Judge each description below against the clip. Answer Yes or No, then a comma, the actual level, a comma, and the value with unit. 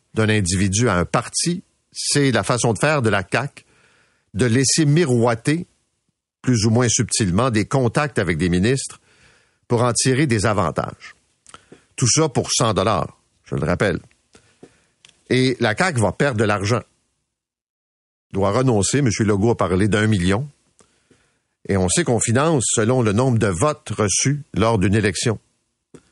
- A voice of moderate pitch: No, low, 115 Hz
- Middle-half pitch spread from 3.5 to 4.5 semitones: Yes, average, 4.2 semitones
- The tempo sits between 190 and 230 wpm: No, average, 155 wpm